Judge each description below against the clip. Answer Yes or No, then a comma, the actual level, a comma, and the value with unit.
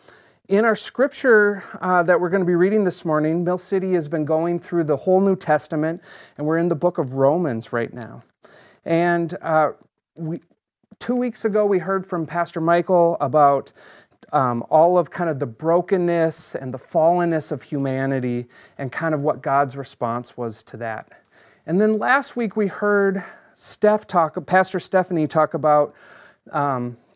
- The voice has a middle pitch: Yes, medium, 170 Hz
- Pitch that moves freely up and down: No, average, 3.8 semitones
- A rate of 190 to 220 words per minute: No, average, 170 wpm